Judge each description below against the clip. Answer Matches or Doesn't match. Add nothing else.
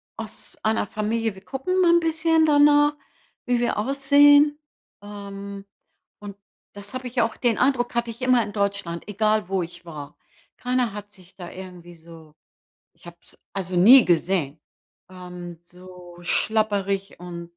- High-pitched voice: Matches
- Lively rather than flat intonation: Matches